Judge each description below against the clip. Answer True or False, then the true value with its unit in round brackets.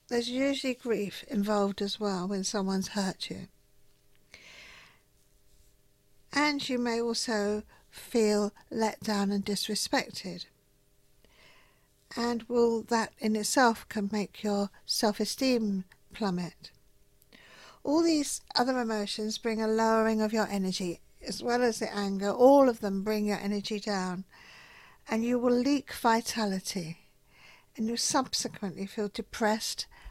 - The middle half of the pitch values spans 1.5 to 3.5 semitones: True (2.9 semitones)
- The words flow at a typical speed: False (120 wpm)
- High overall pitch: True (215 Hz)